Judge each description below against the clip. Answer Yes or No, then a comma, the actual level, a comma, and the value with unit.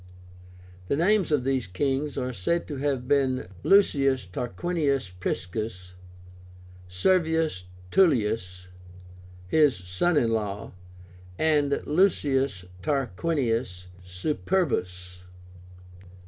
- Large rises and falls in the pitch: Yes, wide, 8.6 semitones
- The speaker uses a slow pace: Yes, slow, 85 wpm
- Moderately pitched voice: No, low, 130 Hz